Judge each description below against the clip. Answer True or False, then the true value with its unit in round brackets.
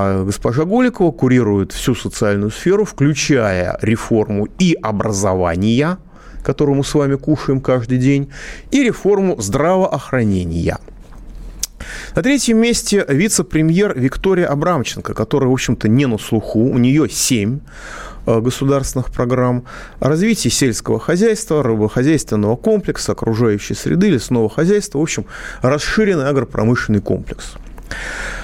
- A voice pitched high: False (130 Hz)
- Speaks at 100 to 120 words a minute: True (110 wpm)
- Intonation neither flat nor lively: False (6.9 semitones)